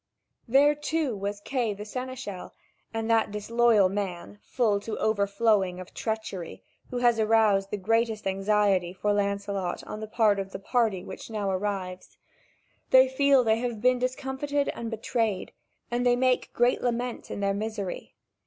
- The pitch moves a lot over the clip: No, average, 3.4 semitones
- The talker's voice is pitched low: No, high, 220 Hz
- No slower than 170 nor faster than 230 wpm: No, average, 155 wpm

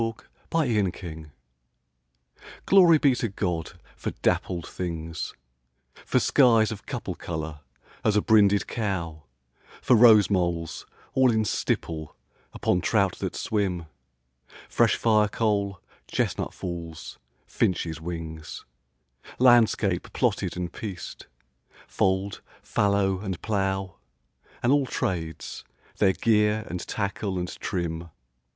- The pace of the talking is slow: Yes, slow, 110 wpm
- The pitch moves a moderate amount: Yes, average, 4.1 semitones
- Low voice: Yes, very low, 95 Hz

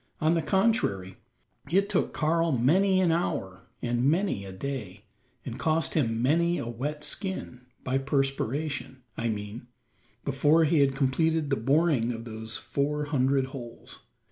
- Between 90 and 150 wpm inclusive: Yes, average, 145 wpm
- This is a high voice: No, medium, 140 Hz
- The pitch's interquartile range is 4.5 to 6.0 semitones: Yes, average, 5.2 semitones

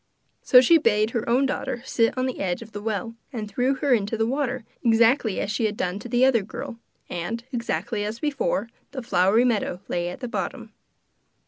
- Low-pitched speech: No, high, 230 Hz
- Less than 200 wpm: No, fast, 205 wpm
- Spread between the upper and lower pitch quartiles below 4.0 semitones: Yes, average, 3.2 semitones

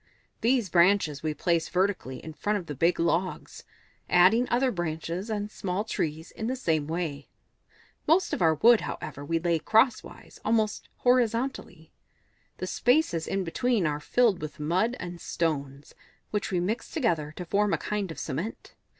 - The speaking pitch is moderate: Yes, medium, 180 Hz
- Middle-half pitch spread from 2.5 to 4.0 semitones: No, wide, 5.5 semitones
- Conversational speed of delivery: Yes, average, 165 wpm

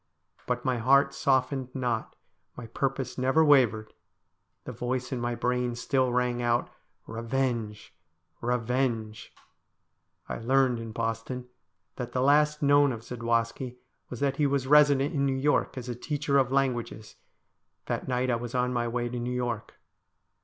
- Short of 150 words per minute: No, average, 160 wpm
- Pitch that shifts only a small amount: Yes, narrow, 2.3 semitones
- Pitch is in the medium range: No, low, 125 Hz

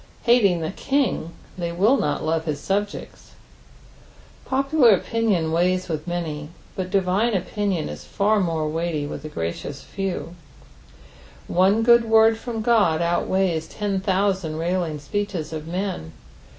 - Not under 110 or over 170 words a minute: Yes, slow, 135 wpm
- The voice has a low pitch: No, medium, 185 Hz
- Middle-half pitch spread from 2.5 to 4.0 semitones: No, average, 4.4 semitones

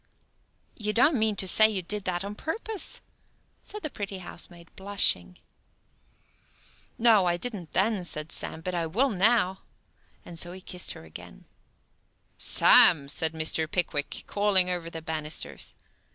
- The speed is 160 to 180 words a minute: No, average, 140 wpm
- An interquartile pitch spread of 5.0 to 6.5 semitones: No, average, 4.2 semitones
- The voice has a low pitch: No, medium, 185 Hz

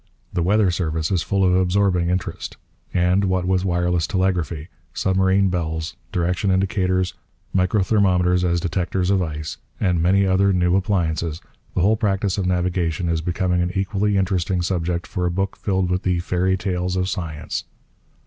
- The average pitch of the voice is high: No, very low, 90 Hz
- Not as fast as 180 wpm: Yes, average, 160 wpm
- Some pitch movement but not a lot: No, narrow, 1.6 semitones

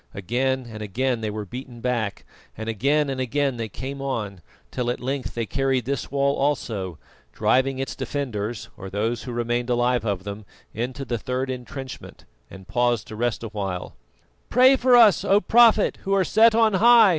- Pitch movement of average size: Yes, average, 4.1 semitones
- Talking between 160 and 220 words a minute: Yes, average, 180 wpm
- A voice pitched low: Yes, low, 125 Hz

